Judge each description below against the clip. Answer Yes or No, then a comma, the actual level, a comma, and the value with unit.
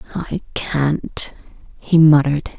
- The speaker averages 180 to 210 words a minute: No, slow, 95 wpm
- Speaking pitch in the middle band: Yes, medium, 155 Hz